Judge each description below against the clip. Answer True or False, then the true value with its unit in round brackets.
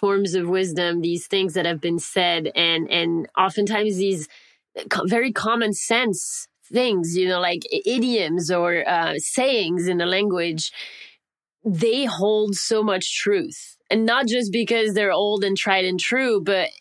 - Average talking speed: True (155 wpm)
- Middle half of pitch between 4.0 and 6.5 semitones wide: True (4.4 semitones)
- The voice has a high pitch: True (195 Hz)